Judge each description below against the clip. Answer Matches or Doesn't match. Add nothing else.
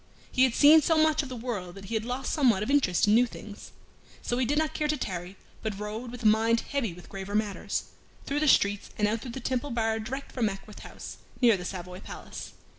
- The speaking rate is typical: Doesn't match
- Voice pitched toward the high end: Matches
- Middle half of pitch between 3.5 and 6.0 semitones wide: Matches